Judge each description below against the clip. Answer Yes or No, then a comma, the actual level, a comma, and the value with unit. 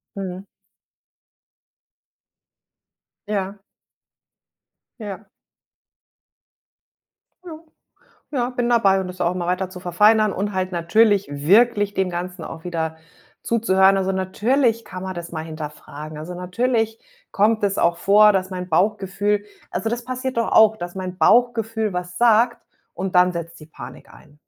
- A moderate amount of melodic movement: Yes, average, 3.6 semitones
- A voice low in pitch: No, high, 190 Hz